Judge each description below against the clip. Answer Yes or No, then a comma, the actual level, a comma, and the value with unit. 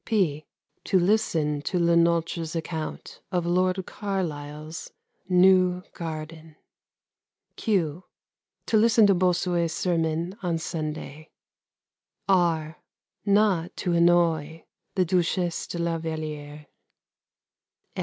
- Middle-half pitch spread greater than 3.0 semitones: No, narrow, 2.5 semitones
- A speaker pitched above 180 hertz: No, medium, 170 Hz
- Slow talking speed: Yes, slow, 95 wpm